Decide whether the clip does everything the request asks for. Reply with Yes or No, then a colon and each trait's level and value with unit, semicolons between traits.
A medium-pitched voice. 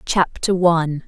Yes: medium, 170 Hz